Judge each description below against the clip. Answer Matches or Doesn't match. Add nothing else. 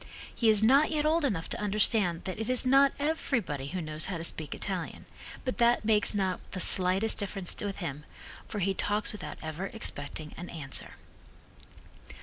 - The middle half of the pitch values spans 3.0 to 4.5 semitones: Doesn't match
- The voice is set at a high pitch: Matches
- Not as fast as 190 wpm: Matches